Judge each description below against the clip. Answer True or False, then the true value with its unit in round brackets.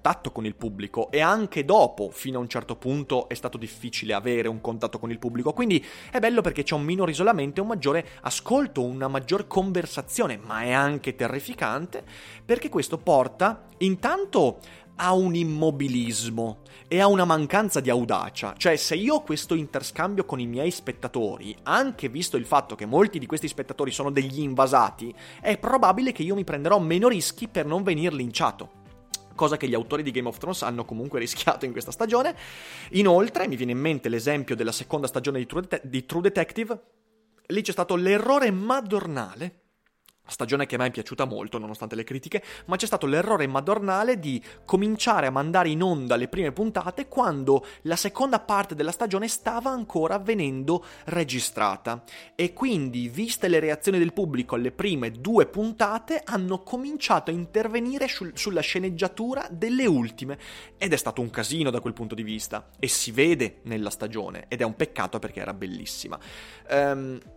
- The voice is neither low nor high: True (160 Hz)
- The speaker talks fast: True (175 wpm)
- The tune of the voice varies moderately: False (8.2 semitones)